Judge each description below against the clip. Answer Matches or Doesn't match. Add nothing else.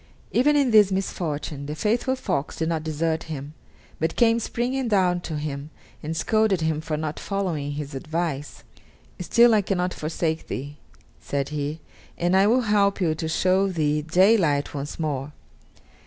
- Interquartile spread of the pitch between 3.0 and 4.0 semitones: Doesn't match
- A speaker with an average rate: Matches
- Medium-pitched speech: Matches